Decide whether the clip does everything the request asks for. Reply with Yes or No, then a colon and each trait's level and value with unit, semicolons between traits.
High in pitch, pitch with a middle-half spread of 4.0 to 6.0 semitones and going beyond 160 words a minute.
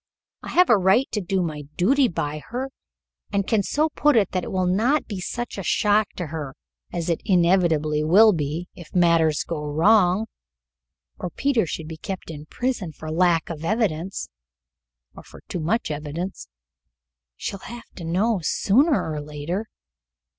No: medium, 180 Hz; average, 5.3 semitones; average, 170 wpm